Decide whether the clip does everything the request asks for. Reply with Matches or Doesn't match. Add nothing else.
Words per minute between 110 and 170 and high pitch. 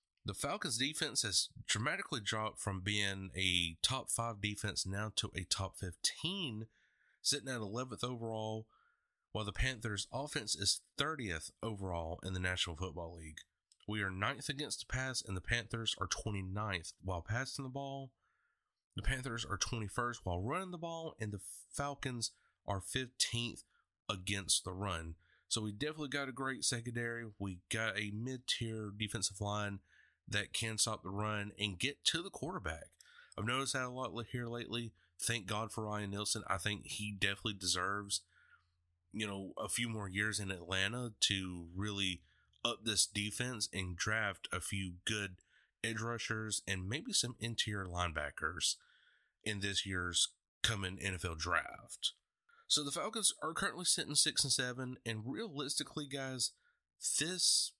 Doesn't match